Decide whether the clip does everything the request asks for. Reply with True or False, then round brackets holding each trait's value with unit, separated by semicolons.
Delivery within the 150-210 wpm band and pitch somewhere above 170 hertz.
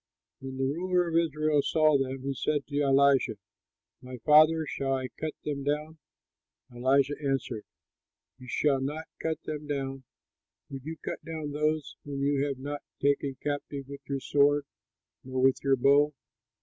False (160 wpm; 140 Hz)